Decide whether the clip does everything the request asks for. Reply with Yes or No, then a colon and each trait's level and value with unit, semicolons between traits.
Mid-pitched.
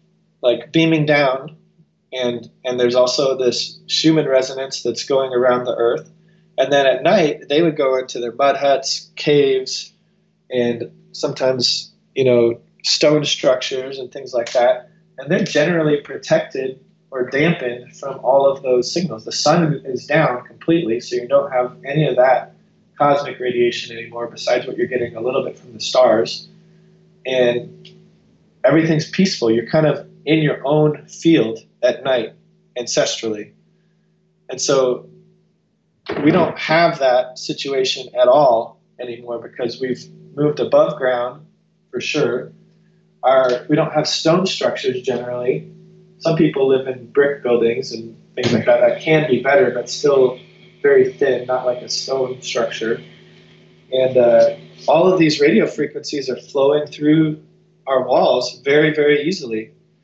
Yes: medium, 150 Hz